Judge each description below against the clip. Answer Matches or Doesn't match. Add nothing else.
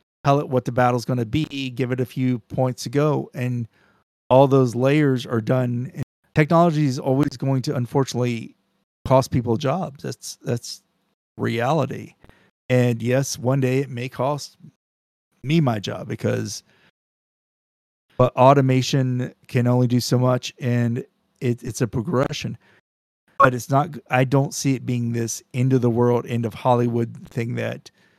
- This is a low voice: Matches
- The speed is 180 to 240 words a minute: Doesn't match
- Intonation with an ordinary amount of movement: Doesn't match